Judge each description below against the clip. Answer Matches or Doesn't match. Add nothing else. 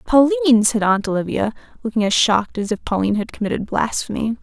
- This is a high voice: Matches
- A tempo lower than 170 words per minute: Doesn't match